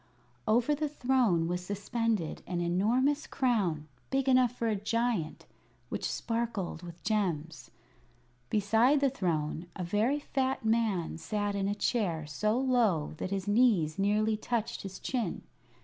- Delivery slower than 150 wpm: Yes, average, 140 wpm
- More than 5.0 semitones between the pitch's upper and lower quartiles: Yes, wide, 5.6 semitones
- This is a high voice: Yes, high, 210 Hz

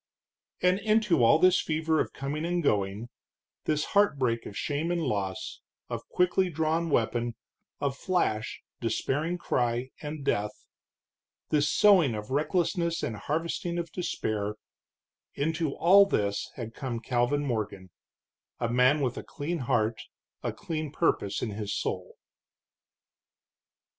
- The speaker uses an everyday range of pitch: No, wide, 6.5 semitones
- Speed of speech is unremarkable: No, slow, 130 wpm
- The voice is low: No, medium, 145 Hz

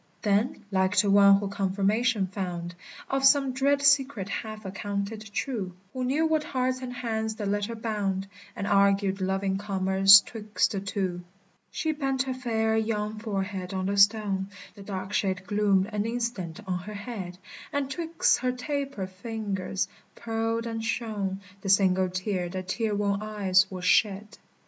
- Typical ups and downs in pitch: Yes, average, 3.1 semitones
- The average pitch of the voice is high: Yes, high, 205 Hz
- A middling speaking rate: Yes, average, 160 wpm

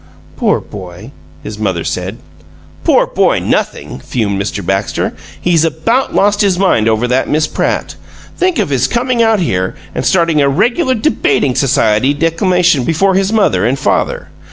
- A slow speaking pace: No, average, 155 wpm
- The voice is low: No, medium, 145 Hz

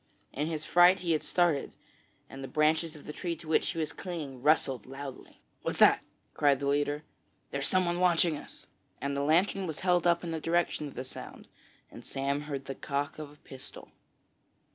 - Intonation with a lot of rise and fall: No, average, 3.4 semitones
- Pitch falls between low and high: Yes, medium, 150 Hz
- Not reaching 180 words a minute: No, average, 195 wpm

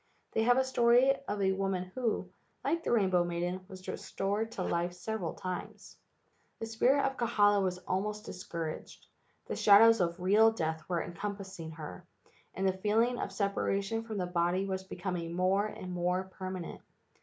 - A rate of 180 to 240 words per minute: No, average, 165 wpm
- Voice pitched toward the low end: No, high, 190 Hz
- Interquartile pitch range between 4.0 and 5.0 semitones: No, average, 3.4 semitones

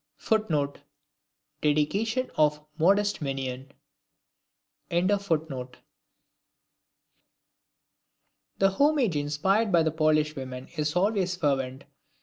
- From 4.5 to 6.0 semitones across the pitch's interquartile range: Yes, average, 5.2 semitones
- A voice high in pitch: No, medium, 155 Hz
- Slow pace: Yes, slow, 75 wpm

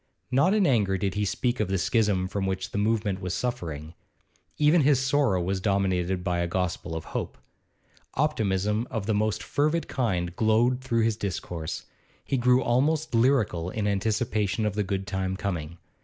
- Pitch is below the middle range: Yes, low, 105 Hz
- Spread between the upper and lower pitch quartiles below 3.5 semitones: No, average, 4.7 semitones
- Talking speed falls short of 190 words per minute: Yes, average, 175 wpm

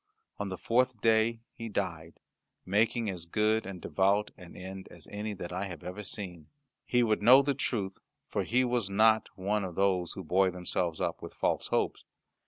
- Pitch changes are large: No, average, 3.4 semitones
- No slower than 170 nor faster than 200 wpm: Yes, average, 190 wpm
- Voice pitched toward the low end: Yes, low, 100 Hz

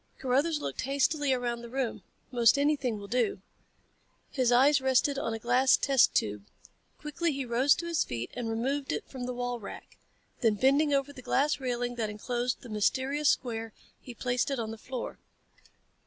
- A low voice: No, very high, 250 Hz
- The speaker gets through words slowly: No, average, 180 wpm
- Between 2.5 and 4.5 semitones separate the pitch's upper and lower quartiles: Yes, average, 2.8 semitones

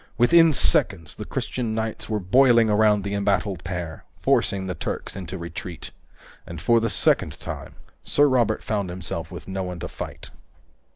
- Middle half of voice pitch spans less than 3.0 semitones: No, average, 4.1 semitones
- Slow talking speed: No, average, 165 wpm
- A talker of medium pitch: No, low, 100 Hz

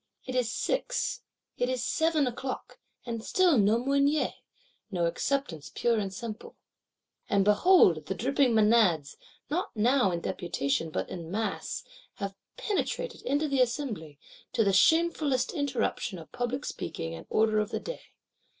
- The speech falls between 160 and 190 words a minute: No, average, 145 wpm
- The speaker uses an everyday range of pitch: No, wide, 6.1 semitones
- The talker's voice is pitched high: Yes, high, 235 Hz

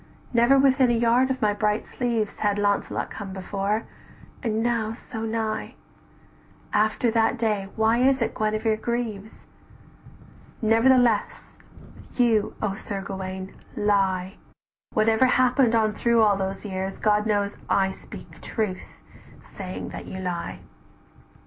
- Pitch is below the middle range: No, high, 215 Hz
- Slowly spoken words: Yes, slow, 130 wpm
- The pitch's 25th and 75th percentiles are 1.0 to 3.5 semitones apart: Yes, average, 2.7 semitones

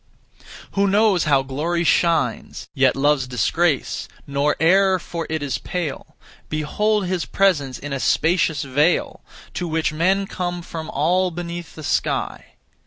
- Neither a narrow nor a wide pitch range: Yes, average, 3.8 semitones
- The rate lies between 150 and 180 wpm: No, average, 140 wpm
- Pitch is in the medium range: Yes, medium, 165 Hz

